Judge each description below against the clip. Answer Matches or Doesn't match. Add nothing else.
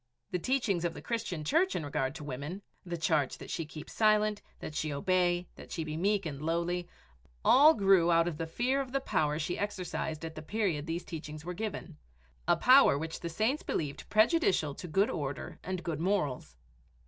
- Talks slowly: Doesn't match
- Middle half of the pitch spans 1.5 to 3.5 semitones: Doesn't match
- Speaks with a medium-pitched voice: Matches